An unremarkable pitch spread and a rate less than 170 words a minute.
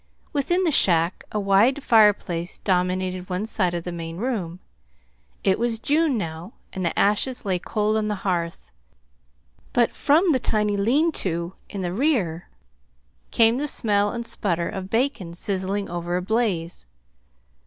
Yes: average, 4.7 semitones; average, 155 wpm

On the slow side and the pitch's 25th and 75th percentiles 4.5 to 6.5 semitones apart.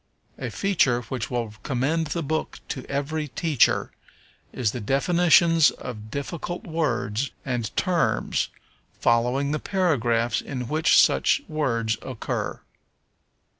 Yes: slow, 115 wpm; average, 5.0 semitones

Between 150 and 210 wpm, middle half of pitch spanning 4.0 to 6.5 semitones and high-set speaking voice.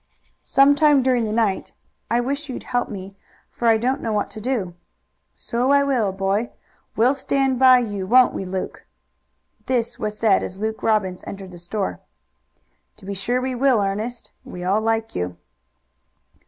Yes: average, 170 wpm; average, 4.5 semitones; high, 225 Hz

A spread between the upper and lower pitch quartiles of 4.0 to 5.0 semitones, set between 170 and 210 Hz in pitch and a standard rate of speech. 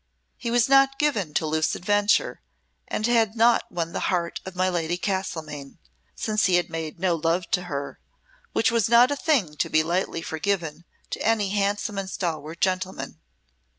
Yes: average, 4.6 semitones; medium, 185 Hz; average, 175 wpm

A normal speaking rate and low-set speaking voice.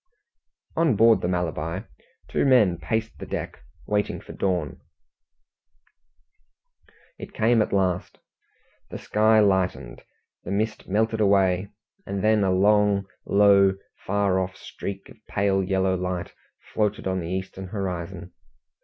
No: slow, 125 wpm; very low, 95 Hz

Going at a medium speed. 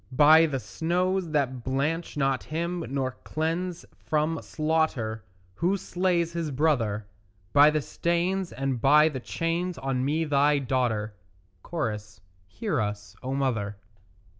No: slow, 130 wpm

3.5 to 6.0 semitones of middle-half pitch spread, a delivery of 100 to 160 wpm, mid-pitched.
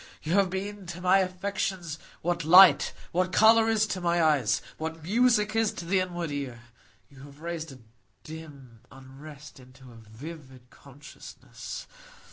Yes: average, 5.2 semitones; average, 150 wpm; medium, 165 Hz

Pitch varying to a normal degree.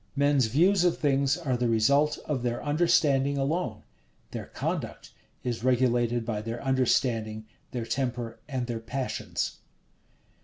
Yes: average, 3.1 semitones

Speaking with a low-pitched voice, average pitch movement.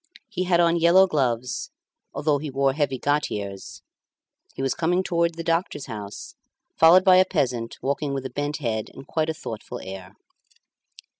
No: medium, 145 Hz; average, 4.9 semitones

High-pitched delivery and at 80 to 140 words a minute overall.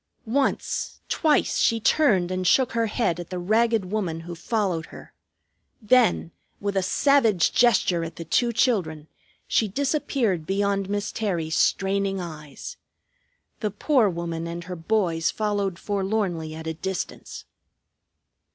Yes: high, 195 Hz; slow, 135 wpm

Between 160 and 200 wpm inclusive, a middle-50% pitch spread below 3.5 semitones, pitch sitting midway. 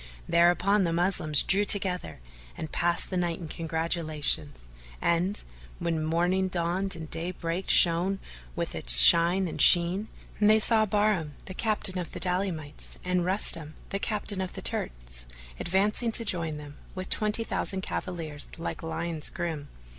No: average, 145 wpm; average, 3.0 semitones; medium, 175 Hz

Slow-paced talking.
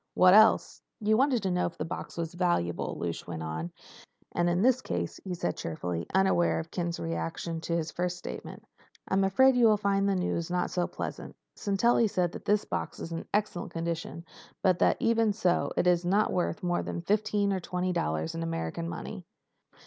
No: average, 195 wpm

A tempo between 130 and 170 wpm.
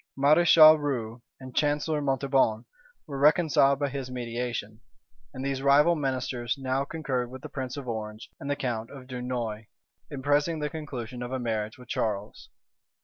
Yes: average, 160 wpm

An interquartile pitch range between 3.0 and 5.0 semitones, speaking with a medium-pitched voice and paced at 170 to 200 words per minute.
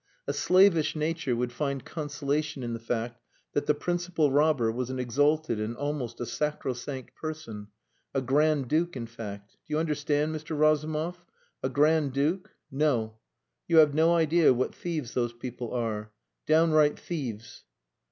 No: average, 4.3 semitones; medium, 145 Hz; average, 150 wpm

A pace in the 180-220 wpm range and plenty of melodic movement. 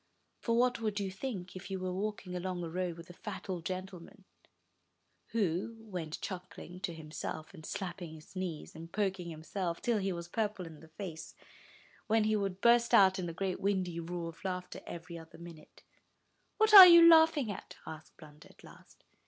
No: average, 185 wpm; average, 3.4 semitones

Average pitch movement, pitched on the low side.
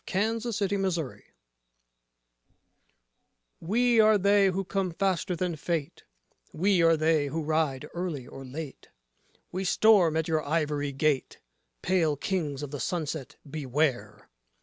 No: average, 4.4 semitones; medium, 165 Hz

